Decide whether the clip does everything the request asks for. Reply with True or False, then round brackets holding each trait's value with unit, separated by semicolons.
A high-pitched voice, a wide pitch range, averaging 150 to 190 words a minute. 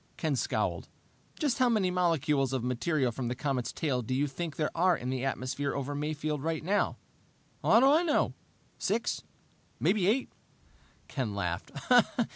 False (150 Hz; 5.9 semitones; 160 wpm)